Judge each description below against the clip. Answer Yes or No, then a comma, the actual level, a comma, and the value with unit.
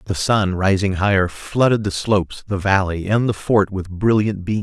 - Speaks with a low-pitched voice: Yes, low, 100 Hz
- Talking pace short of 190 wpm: No, average, 195 wpm